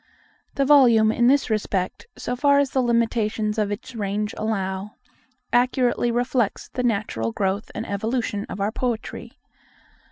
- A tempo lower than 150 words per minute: Yes, average, 140 wpm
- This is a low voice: No, high, 225 Hz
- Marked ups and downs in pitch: No, average, 3.2 semitones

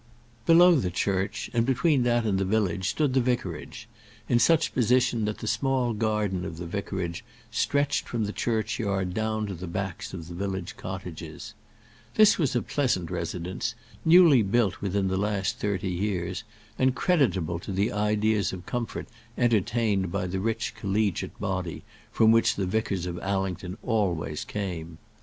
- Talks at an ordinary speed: Yes, average, 160 wpm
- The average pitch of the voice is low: Yes, low, 100 Hz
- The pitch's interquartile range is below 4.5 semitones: Yes, average, 4.1 semitones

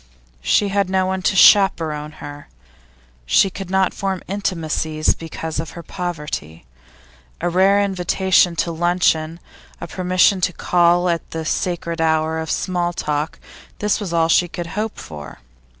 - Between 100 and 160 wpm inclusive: Yes, average, 150 wpm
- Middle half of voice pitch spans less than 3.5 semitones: Yes, average, 2.8 semitones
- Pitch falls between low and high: Yes, medium, 175 Hz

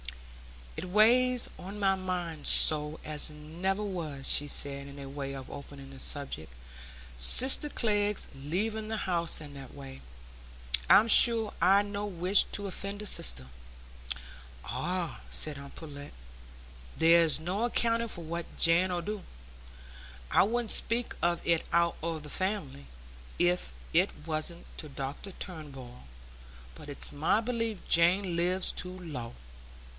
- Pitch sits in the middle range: Yes, medium, 170 Hz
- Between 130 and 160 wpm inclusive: Yes, average, 140 wpm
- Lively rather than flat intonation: Yes, wide, 5.7 semitones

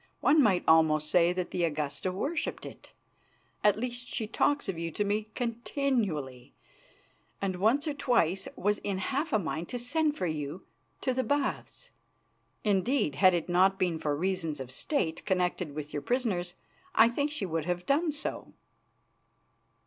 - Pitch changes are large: Yes, wide, 6.9 semitones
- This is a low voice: No, high, 190 Hz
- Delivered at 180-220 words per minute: No, average, 165 wpm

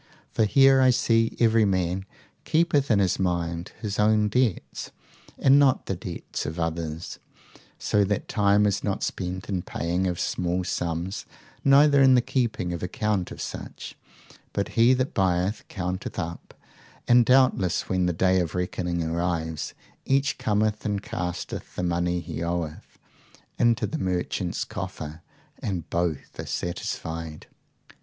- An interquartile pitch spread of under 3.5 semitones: No, average, 4.2 semitones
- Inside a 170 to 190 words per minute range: No, average, 145 wpm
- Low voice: Yes, very low, 95 Hz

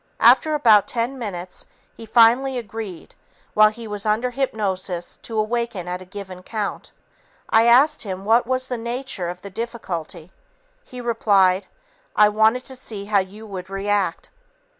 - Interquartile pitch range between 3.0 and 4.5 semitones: Yes, average, 3.6 semitones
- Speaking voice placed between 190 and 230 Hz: Yes, high, 215 Hz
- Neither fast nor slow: Yes, average, 155 wpm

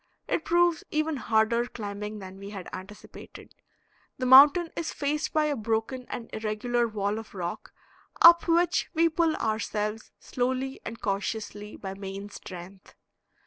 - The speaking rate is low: No, average, 145 wpm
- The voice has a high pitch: Yes, high, 225 Hz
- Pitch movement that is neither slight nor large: No, wide, 6.1 semitones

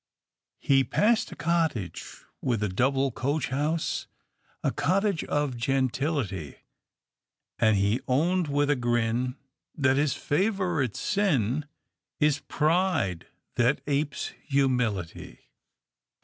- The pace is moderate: No, slow, 105 wpm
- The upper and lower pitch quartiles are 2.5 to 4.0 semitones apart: No, average, 4.5 semitones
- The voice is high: No, medium, 140 Hz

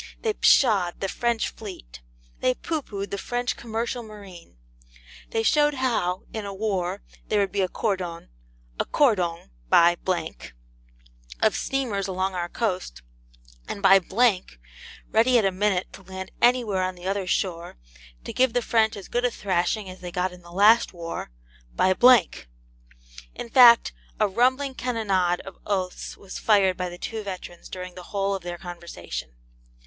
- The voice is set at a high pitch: Yes, high, 195 Hz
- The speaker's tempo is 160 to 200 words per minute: Yes, average, 165 wpm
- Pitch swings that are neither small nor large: Yes, average, 4.0 semitones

